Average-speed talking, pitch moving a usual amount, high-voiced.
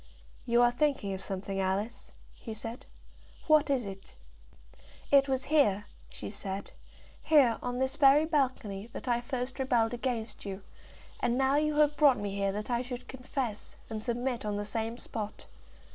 Yes: average, 165 wpm; average, 4.4 semitones; high, 240 Hz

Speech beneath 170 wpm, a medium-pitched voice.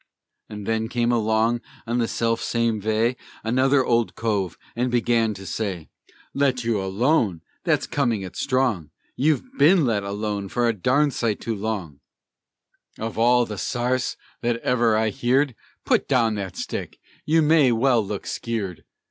No: average, 155 wpm; low, 115 Hz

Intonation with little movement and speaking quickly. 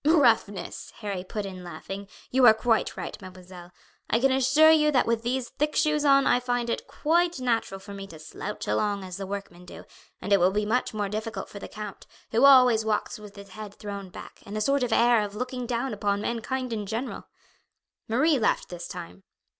No: average, 4.1 semitones; fast, 210 wpm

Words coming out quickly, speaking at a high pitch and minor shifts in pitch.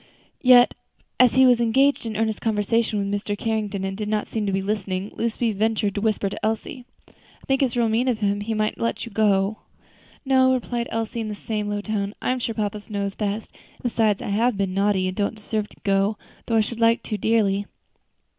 Yes: fast, 220 wpm; high, 215 Hz; narrow, 2.2 semitones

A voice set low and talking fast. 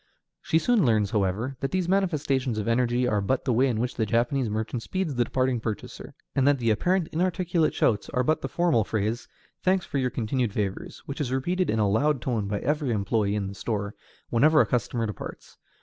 Yes: low, 125 Hz; fast, 210 wpm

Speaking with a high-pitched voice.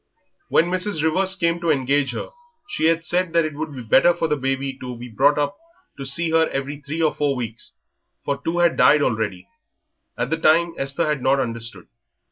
No: medium, 145 Hz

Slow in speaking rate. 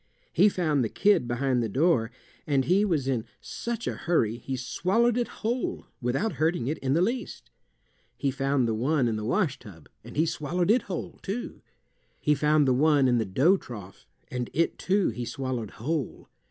No: average, 190 wpm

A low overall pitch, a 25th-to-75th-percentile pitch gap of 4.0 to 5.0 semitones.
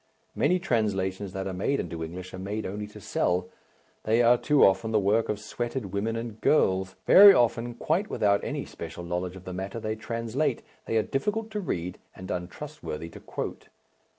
Yes: low, 105 Hz; average, 4.3 semitones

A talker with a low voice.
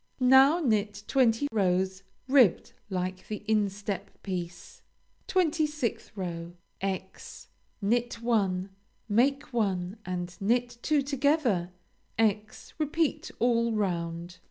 No: high, 210 Hz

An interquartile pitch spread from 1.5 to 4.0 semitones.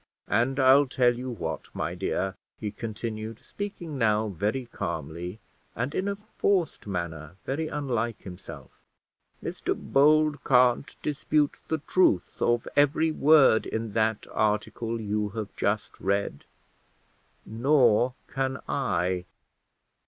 No: average, 5.1 semitones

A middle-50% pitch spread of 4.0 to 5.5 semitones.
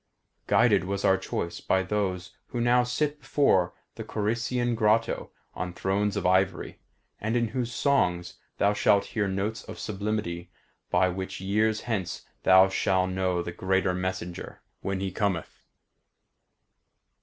No: average, 3.0 semitones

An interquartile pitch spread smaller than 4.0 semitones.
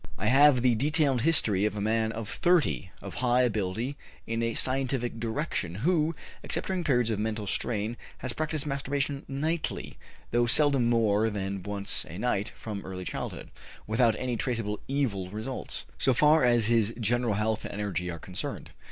No: average, 4.5 semitones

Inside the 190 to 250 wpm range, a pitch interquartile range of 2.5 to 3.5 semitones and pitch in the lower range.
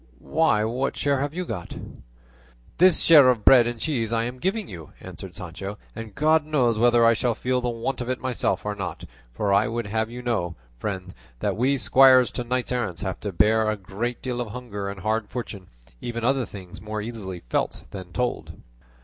No: fast, 205 wpm; average, 4.0 semitones; low, 115 Hz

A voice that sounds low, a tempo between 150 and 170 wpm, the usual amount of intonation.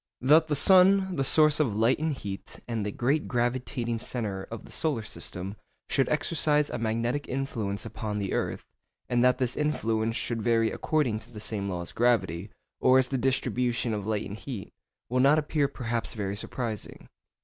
No: low, 120 Hz; average, 180 wpm; average, 4.2 semitones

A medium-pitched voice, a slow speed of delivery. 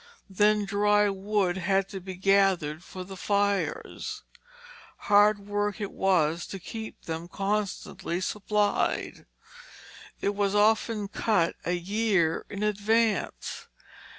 No: high, 200 Hz; slow, 115 wpm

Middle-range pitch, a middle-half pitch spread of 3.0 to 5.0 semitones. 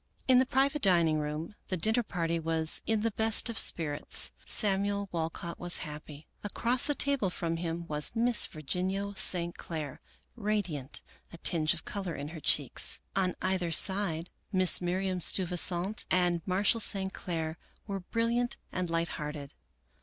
Yes: medium, 180 Hz; average, 3.9 semitones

